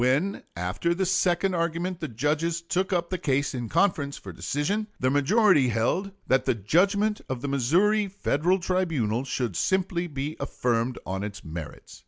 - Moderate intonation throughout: No, wide, 6.5 semitones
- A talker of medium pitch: Yes, medium, 155 Hz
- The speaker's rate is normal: Yes, average, 165 wpm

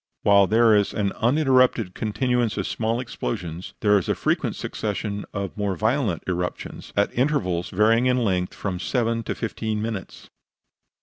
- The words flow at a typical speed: Yes, average, 150 wpm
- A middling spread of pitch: Yes, average, 3.3 semitones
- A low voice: Yes, low, 105 Hz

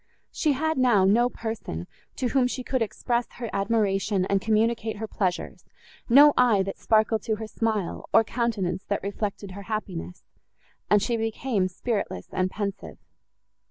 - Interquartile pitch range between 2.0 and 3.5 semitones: Yes, average, 3.2 semitones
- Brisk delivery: No, average, 155 wpm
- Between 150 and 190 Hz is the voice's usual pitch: No, high, 215 Hz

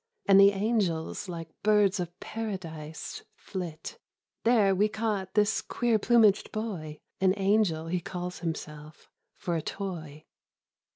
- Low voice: No, high, 190 Hz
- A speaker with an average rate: No, slow, 125 wpm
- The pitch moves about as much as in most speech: Yes, average, 4.3 semitones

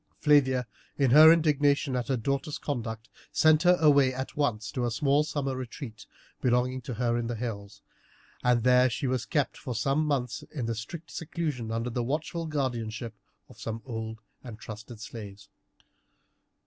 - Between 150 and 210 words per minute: Yes, average, 160 wpm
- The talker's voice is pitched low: Yes, low, 125 Hz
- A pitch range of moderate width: Yes, average, 4.0 semitones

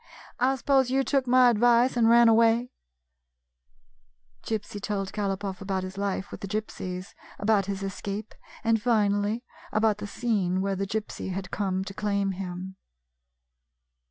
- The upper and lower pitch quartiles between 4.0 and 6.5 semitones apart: No, average, 3.1 semitones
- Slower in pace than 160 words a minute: Yes, average, 150 wpm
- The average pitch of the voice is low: No, high, 205 Hz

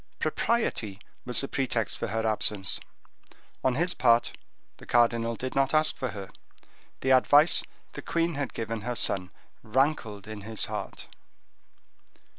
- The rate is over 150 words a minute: No, average, 140 wpm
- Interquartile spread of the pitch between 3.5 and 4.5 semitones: Yes, average, 4.0 semitones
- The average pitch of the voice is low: Yes, low, 120 Hz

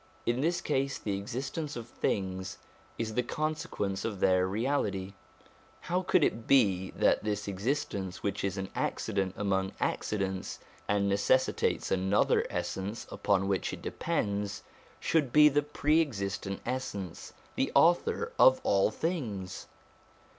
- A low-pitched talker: Yes, low, 100 Hz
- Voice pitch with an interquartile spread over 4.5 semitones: Yes, wide, 5.4 semitones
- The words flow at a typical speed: No, slow, 130 wpm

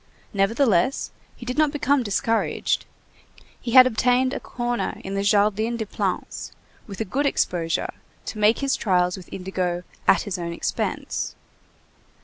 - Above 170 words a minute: No, average, 145 wpm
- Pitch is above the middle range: Yes, high, 215 Hz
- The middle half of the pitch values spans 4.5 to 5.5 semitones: Yes, average, 4.8 semitones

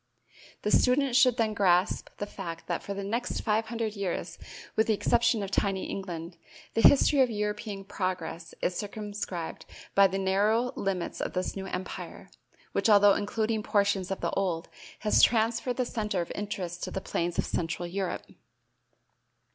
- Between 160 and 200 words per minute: Yes, average, 165 wpm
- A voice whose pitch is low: No, high, 200 Hz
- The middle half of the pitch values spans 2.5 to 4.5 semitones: Yes, average, 2.8 semitones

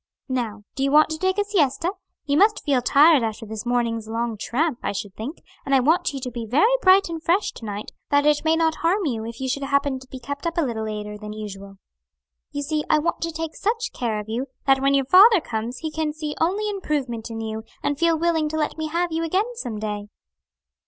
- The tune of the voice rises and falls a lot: Yes, wide, 6.1 semitones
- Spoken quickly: Yes, fast, 240 wpm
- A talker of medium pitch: No, very high, 280 Hz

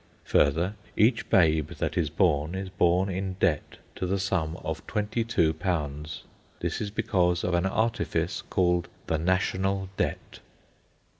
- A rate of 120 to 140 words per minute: Yes, slow, 135 wpm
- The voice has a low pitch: Yes, very low, 90 Hz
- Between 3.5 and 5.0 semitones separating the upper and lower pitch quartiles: No, average, 3.1 semitones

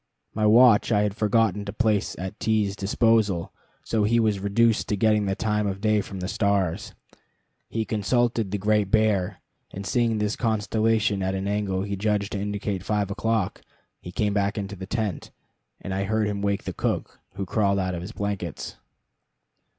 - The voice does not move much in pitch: Yes, narrow, 1.9 semitones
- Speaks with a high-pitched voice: No, low, 105 Hz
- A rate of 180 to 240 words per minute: Yes, average, 185 wpm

